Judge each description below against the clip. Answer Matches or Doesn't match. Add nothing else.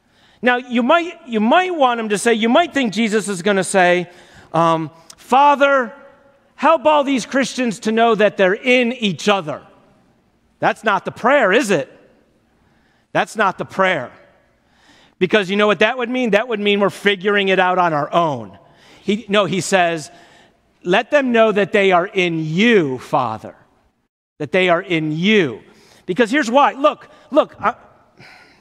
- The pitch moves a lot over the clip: Matches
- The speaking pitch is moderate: Doesn't match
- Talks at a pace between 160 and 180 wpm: Matches